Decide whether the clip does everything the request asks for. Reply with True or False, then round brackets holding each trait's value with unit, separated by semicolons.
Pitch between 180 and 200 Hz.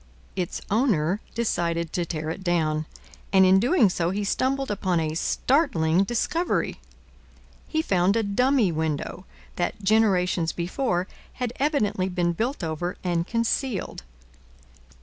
True (190 Hz)